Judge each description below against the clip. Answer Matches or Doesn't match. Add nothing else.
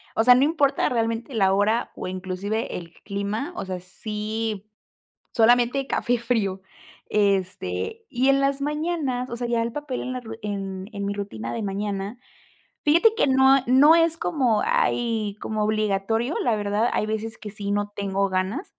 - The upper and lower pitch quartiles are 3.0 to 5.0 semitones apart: Matches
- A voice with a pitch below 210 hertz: Doesn't match